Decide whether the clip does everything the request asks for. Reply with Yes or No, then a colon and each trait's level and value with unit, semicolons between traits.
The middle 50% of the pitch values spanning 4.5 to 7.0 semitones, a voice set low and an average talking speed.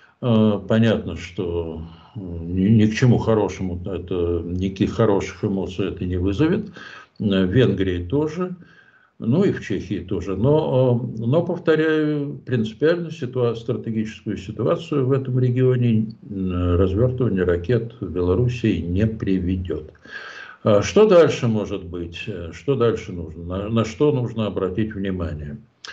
Yes: average, 5.2 semitones; low, 110 Hz; average, 120 wpm